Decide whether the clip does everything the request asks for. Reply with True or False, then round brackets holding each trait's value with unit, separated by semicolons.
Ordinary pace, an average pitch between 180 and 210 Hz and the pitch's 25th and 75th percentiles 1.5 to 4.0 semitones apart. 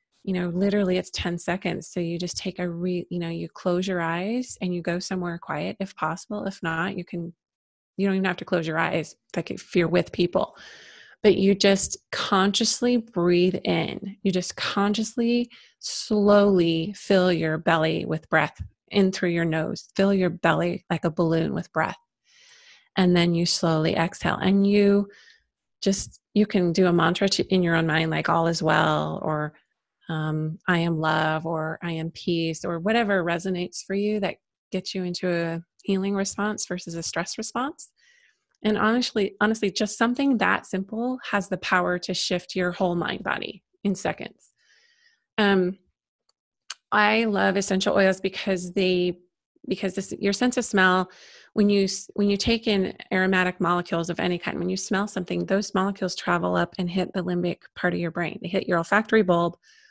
True (180 wpm; 185 Hz; 2.8 semitones)